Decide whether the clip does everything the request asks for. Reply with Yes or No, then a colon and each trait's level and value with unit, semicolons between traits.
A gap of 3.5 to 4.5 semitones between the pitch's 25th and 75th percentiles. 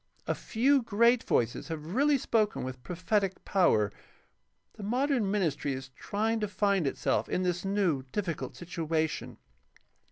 No: wide, 5.5 semitones